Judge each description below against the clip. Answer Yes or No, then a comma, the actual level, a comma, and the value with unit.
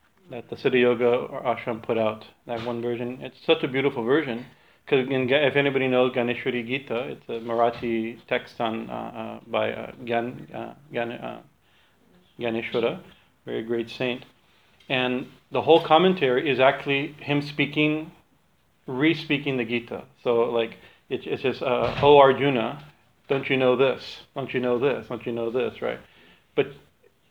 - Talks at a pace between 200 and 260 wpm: No, average, 155 wpm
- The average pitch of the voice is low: Yes, low, 125 Hz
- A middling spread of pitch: Yes, average, 3.0 semitones